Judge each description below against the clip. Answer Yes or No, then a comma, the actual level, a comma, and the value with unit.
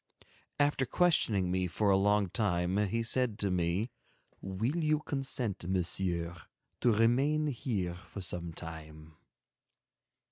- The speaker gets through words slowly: Yes, slow, 120 wpm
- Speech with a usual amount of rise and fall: No, wide, 5.8 semitones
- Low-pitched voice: Yes, low, 100 Hz